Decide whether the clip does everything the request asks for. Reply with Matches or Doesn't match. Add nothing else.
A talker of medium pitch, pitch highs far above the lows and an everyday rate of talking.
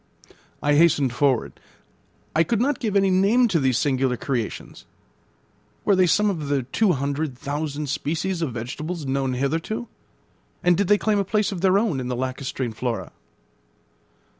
Matches